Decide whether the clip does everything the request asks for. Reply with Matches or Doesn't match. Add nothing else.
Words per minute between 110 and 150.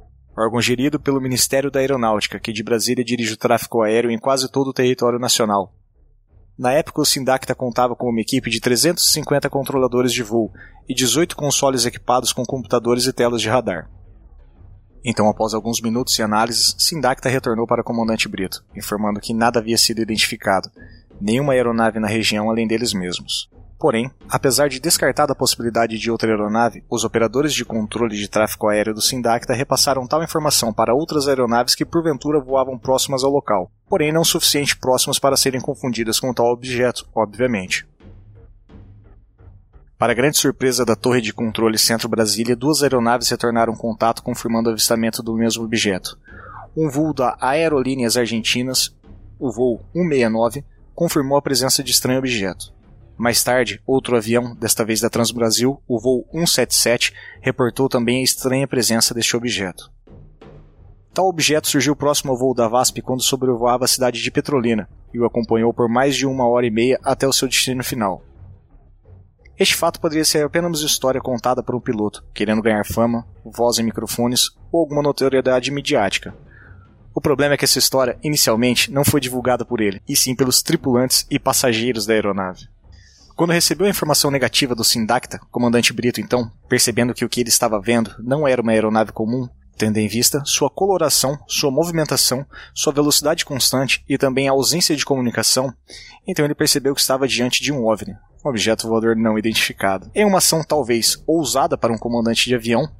Doesn't match